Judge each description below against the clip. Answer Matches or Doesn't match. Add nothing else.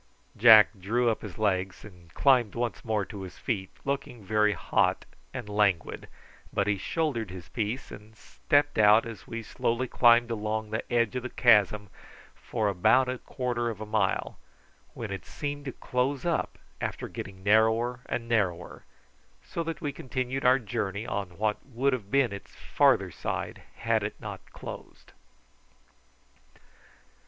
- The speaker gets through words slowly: Doesn't match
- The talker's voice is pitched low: Matches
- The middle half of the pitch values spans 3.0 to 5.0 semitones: Matches